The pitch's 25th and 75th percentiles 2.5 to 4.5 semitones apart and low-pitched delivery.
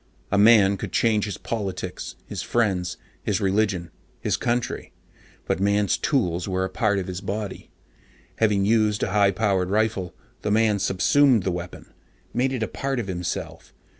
Yes: average, 2.8 semitones; low, 100 Hz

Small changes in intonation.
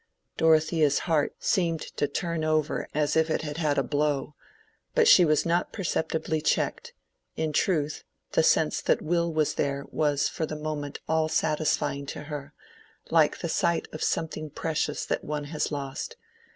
Yes: narrow, 1.7 semitones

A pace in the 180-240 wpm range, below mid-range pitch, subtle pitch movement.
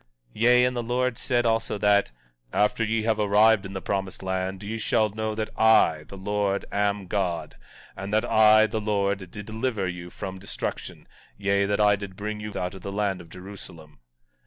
Yes: average, 195 wpm; low, 105 Hz; narrow, 2.2 semitones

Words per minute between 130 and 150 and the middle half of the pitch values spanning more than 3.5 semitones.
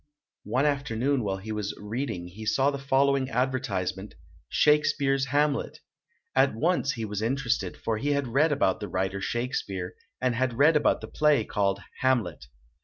No: average, 160 wpm; average, 5.1 semitones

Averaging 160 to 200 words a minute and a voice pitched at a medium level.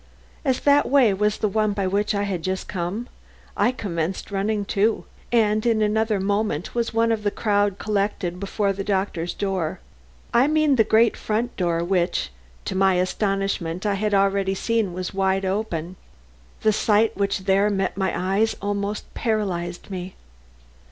No: average, 165 wpm; high, 200 Hz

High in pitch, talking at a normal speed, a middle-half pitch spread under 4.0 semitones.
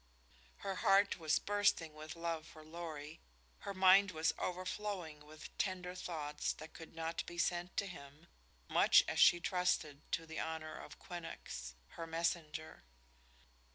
No: medium, 165 Hz; average, 145 wpm; narrow, 2.5 semitones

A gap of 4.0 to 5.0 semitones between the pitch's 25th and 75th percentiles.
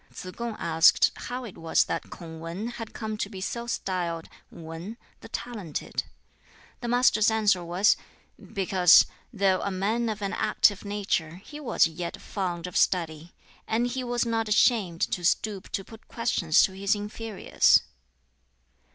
Yes: average, 4.4 semitones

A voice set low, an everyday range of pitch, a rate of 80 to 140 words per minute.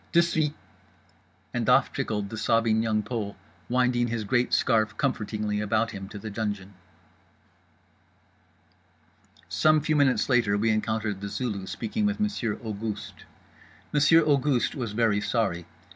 Yes: low, 110 Hz; average, 3.5 semitones; slow, 135 wpm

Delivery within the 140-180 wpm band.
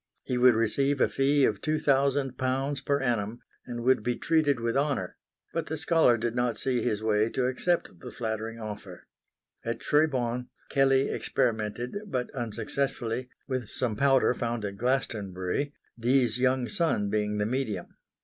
Yes: average, 160 wpm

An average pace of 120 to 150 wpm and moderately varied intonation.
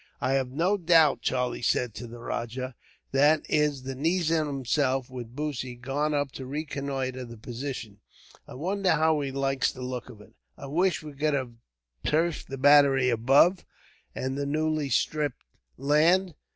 No: average, 165 wpm; average, 3.0 semitones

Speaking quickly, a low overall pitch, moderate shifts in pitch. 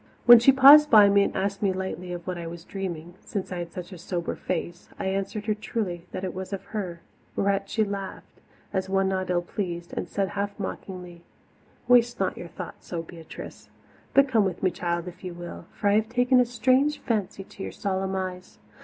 No: fast, 215 wpm; high, 190 Hz; average, 3.1 semitones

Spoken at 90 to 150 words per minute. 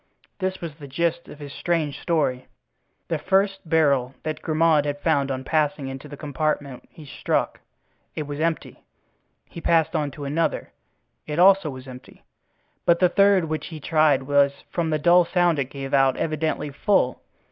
No: average, 165 wpm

